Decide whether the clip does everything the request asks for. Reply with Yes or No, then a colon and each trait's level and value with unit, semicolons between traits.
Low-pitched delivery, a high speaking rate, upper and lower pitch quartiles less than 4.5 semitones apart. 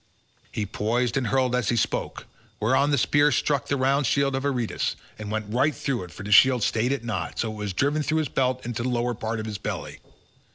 Yes: low, 125 Hz; fast, 240 wpm; average, 3.9 semitones